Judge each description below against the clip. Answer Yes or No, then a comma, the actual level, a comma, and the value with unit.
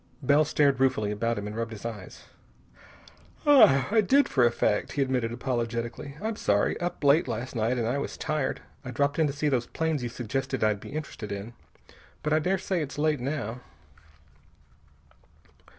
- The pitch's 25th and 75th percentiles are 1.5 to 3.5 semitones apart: No, average, 4.6 semitones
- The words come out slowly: No, average, 175 wpm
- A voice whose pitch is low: Yes, low, 130 Hz